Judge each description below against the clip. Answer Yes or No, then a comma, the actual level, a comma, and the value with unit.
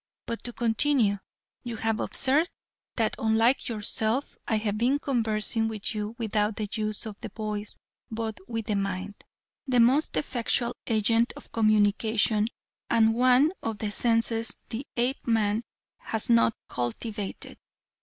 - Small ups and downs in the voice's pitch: Yes, narrow, 1.9 semitones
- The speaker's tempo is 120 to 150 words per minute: Yes, slow, 135 wpm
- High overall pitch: Yes, high, 225 Hz